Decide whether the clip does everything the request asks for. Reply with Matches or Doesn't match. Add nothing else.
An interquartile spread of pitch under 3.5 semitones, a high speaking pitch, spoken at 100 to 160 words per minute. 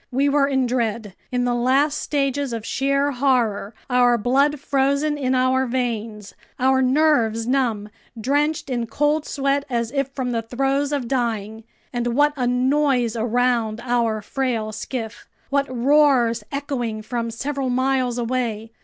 Matches